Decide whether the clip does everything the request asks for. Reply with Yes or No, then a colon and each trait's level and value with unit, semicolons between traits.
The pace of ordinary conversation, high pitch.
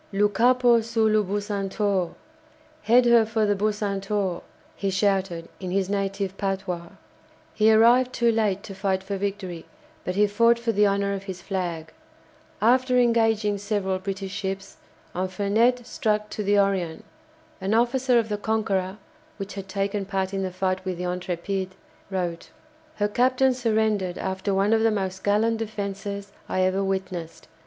Yes: average, 155 wpm; high, 200 Hz